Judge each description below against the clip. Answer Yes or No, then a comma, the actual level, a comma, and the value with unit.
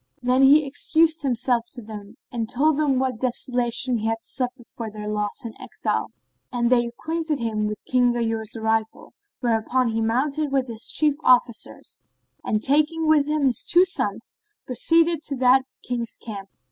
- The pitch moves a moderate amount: Yes, average, 3.8 semitones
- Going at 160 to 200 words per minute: Yes, average, 165 wpm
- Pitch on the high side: Yes, high, 245 Hz